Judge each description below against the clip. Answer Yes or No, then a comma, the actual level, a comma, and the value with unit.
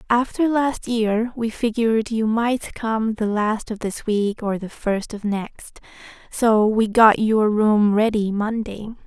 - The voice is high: Yes, high, 220 Hz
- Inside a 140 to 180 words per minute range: Yes, average, 165 wpm